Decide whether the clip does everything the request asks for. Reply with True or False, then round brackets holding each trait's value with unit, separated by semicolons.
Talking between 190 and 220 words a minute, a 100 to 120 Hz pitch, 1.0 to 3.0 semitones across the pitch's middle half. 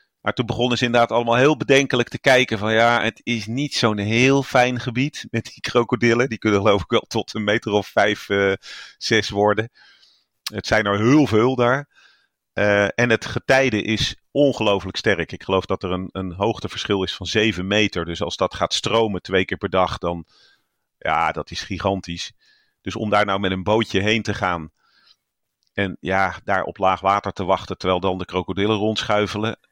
False (195 wpm; 105 Hz; 3.8 semitones)